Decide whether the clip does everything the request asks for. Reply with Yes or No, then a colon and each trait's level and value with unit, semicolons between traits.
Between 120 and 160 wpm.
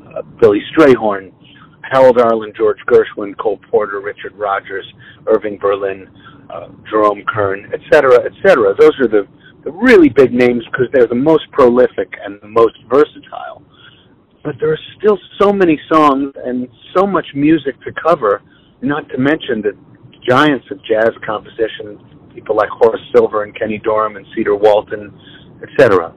Yes: average, 150 wpm